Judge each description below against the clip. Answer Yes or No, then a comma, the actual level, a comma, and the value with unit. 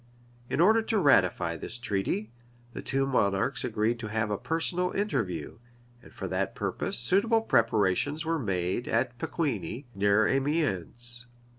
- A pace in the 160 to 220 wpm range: No, average, 145 wpm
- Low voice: Yes, low, 120 Hz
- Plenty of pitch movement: Yes, wide, 6.7 semitones